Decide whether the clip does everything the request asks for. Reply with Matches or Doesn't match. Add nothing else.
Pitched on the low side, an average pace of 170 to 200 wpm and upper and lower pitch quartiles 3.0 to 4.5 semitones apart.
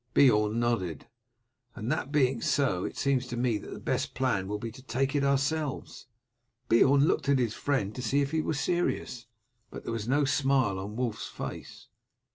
Matches